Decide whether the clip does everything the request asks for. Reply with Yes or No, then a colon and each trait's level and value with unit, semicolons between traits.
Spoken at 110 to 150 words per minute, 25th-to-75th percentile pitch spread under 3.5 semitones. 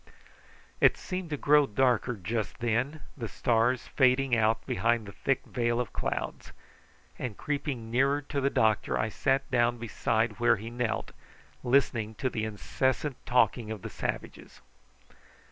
Yes: average, 145 wpm; average, 3.1 semitones